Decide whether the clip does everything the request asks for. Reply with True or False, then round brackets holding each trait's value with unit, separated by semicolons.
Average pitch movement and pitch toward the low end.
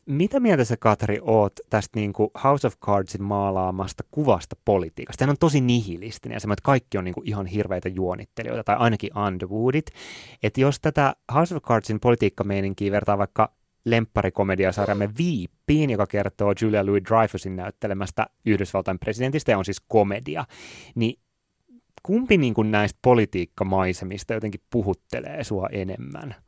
True (3.4 semitones; 105 Hz)